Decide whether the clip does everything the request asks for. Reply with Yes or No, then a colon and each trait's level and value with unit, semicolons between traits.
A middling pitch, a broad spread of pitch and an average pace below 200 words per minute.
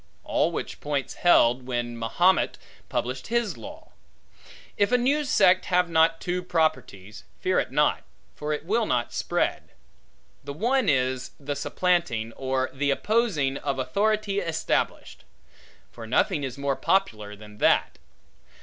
Yes: medium, 145 Hz; wide, 6.7 semitones; average, 140 wpm